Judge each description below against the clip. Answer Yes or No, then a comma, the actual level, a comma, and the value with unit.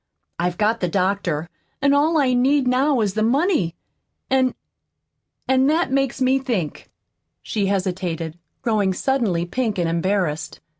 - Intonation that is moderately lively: No, wide, 6.8 semitones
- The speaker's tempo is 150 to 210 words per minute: No, average, 140 wpm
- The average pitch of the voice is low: No, high, 220 Hz